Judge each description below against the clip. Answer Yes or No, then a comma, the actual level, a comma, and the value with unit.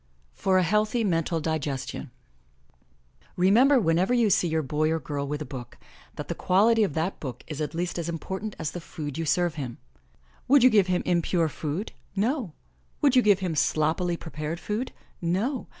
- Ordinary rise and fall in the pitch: Yes, average, 4.9 semitones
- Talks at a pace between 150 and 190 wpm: Yes, average, 180 wpm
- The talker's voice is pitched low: No, medium, 175 Hz